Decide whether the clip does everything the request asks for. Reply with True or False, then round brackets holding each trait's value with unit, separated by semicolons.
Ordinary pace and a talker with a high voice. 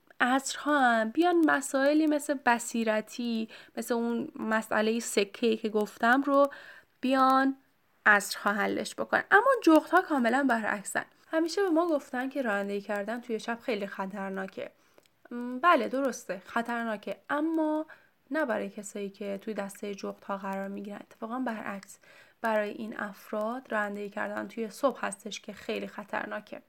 True (140 wpm; 230 Hz)